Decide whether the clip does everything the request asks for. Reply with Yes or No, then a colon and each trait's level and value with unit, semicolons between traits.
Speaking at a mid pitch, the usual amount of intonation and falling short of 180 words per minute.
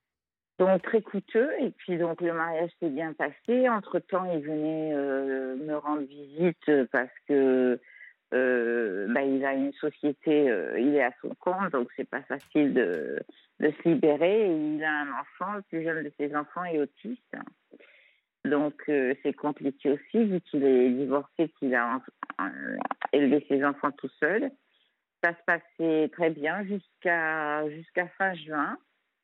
Yes: medium, 150 Hz; average, 4.4 semitones; average, 165 wpm